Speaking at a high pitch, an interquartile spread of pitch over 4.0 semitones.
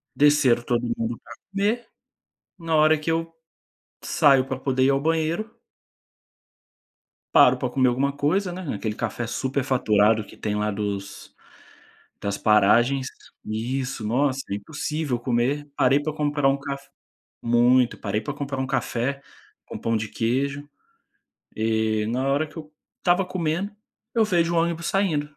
No: low, 135 Hz; average, 4.8 semitones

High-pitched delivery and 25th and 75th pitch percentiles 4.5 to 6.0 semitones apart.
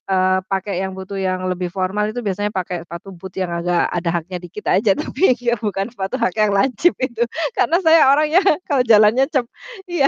Yes: high, 200 Hz; average, 4.8 semitones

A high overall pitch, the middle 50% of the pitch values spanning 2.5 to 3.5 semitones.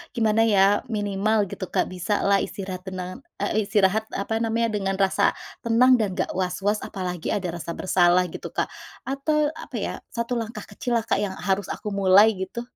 Yes: high, 205 Hz; average, 2.8 semitones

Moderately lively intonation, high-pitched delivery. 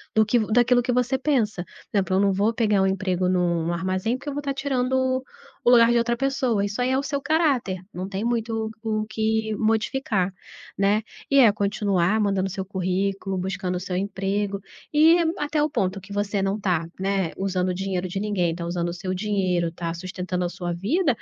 Yes: average, 4.2 semitones; high, 200 Hz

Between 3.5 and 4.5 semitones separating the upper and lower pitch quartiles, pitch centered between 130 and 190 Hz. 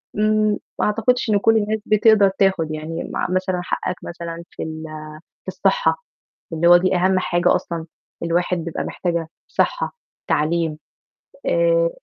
Yes: average, 4.0 semitones; medium, 185 Hz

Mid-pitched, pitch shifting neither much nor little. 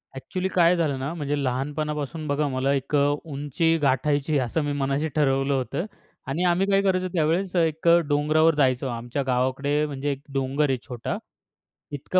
Yes: medium, 145 Hz; average, 3.0 semitones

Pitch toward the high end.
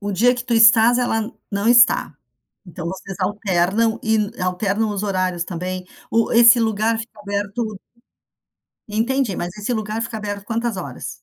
Yes: high, 210 Hz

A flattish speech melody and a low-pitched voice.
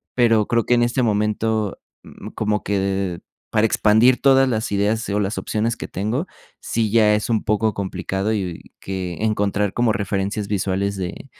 Yes: narrow, 2.2 semitones; low, 105 Hz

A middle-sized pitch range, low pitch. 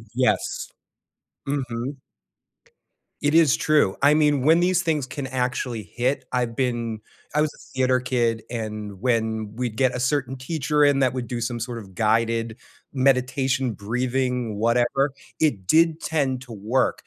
Yes: average, 3.0 semitones; low, 125 Hz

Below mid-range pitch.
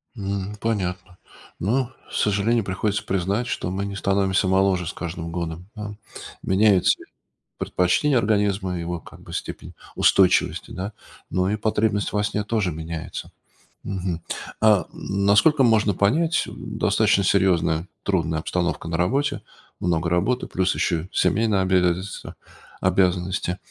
Yes: very low, 95 Hz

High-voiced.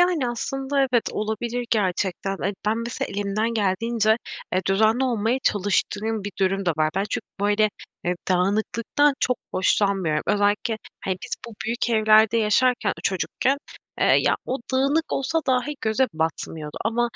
Yes: high, 220 Hz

